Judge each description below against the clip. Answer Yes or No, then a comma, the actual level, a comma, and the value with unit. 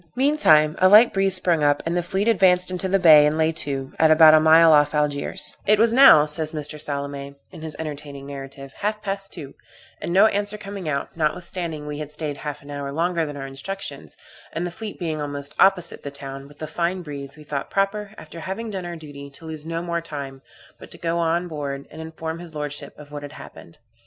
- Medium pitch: Yes, medium, 160 Hz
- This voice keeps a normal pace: No, fast, 220 wpm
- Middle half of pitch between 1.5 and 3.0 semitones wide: No, average, 3.8 semitones